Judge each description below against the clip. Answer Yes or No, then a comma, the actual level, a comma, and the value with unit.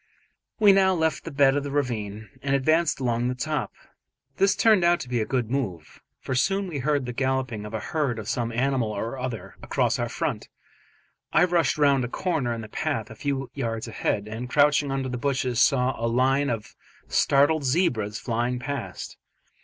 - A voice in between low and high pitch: No, low, 130 Hz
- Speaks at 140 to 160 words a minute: No, average, 195 wpm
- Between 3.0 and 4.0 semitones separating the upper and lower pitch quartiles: Yes, average, 3.7 semitones